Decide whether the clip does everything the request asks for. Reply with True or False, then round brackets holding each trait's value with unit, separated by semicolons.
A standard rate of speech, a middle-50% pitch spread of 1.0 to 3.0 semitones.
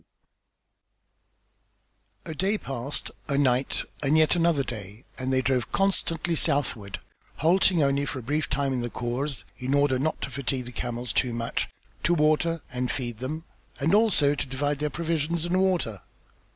False (165 wpm; 4.1 semitones)